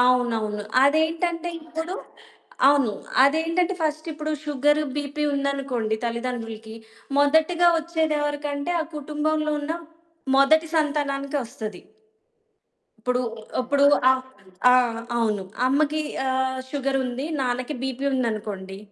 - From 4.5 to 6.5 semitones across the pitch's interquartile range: No, average, 3.7 semitones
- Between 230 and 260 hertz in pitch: No, very high, 280 Hz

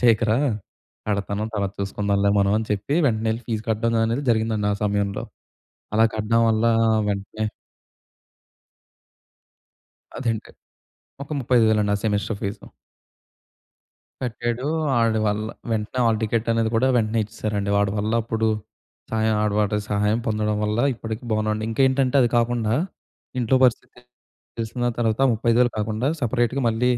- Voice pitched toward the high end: No, low, 110 Hz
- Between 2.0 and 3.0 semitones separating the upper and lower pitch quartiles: No, narrow, 1.6 semitones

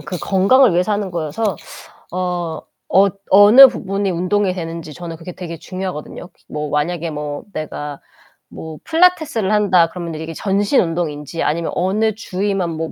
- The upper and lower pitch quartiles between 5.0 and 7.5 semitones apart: No, average, 3.5 semitones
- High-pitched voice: No, medium, 180 Hz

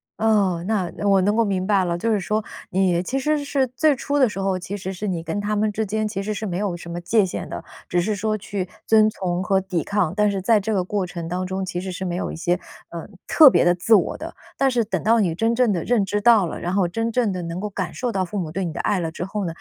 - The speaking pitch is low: No, high, 195 Hz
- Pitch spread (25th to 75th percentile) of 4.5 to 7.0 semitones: No, average, 3.2 semitones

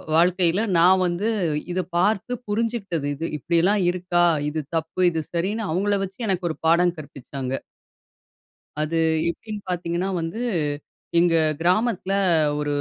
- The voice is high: No, medium, 180 Hz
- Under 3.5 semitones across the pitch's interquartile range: Yes, average, 3.0 semitones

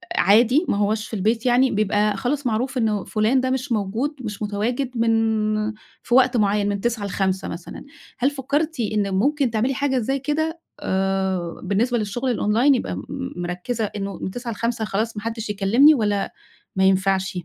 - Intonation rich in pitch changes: No, average, 4.1 semitones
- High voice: Yes, high, 220 Hz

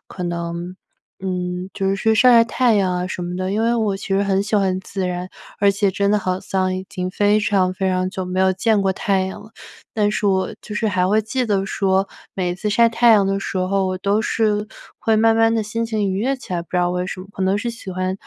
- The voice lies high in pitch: Yes, high, 195 Hz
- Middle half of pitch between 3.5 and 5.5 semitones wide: No, narrow, 2.4 semitones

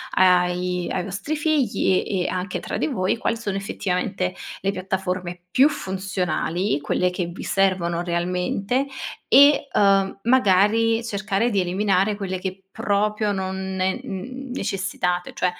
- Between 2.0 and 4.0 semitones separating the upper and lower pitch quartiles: Yes, narrow, 2.5 semitones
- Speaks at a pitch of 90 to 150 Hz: No, high, 190 Hz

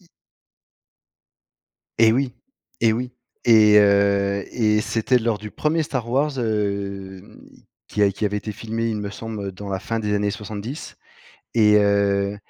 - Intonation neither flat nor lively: No, narrow, 2.2 semitones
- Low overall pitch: Yes, low, 105 Hz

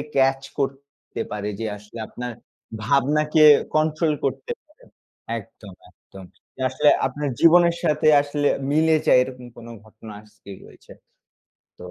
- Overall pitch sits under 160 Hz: Yes, medium, 140 Hz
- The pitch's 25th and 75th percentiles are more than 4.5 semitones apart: Yes, average, 4.9 semitones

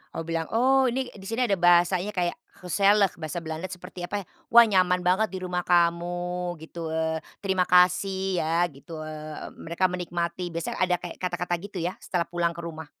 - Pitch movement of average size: No, narrow, 1.9 semitones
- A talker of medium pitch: Yes, medium, 180 Hz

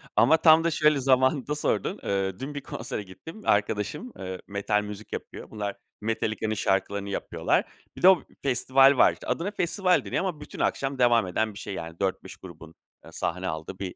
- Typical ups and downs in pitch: No, wide, 6.8 semitones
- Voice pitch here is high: No, low, 110 Hz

